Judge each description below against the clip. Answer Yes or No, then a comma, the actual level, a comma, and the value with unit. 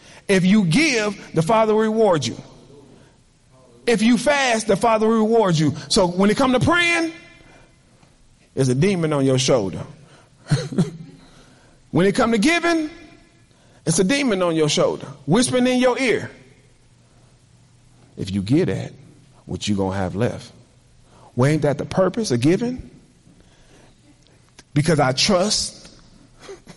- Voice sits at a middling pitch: Yes, medium, 155 Hz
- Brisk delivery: No, average, 140 wpm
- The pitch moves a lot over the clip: Yes, wide, 8.8 semitones